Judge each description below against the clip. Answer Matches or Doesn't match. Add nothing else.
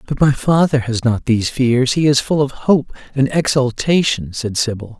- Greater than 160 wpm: Matches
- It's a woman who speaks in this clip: Doesn't match